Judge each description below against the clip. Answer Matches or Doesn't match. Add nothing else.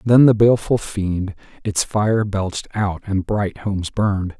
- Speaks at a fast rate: Doesn't match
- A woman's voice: Doesn't match